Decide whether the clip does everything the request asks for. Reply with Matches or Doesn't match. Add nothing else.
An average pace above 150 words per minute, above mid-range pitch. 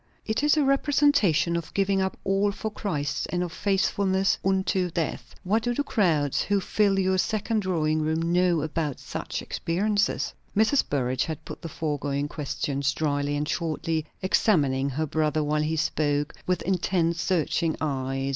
Doesn't match